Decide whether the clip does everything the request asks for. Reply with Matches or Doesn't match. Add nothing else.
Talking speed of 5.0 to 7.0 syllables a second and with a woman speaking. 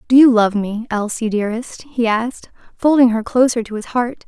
Matches